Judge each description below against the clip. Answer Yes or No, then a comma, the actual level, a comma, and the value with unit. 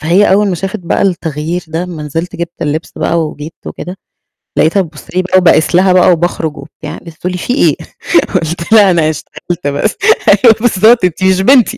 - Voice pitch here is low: No, medium, 175 Hz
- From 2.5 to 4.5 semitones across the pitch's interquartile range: Yes, average, 2.9 semitones